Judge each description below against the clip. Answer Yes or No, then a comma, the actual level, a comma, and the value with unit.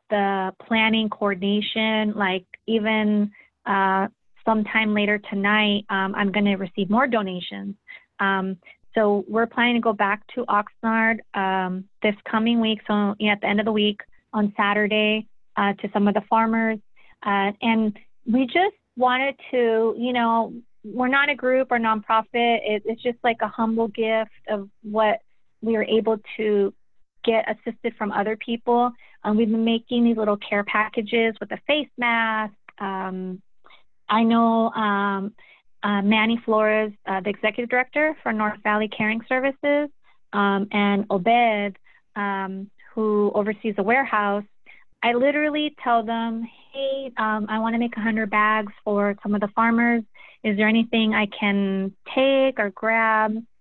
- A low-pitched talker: No, high, 220 Hz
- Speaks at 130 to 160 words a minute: Yes, average, 155 wpm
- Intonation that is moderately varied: No, narrow, 2.0 semitones